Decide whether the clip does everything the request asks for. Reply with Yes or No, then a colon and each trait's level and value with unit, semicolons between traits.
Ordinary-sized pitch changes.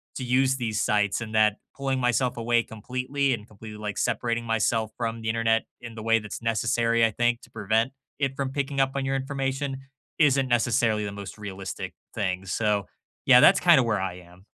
Yes: average, 3.6 semitones